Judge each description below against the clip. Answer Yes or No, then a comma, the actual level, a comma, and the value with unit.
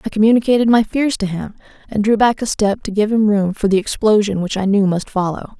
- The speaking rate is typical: No, fast, 245 wpm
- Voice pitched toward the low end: No, high, 210 Hz